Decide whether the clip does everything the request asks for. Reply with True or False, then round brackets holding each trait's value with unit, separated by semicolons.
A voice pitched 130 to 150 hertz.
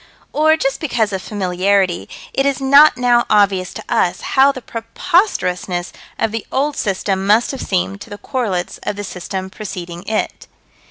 False (210 Hz)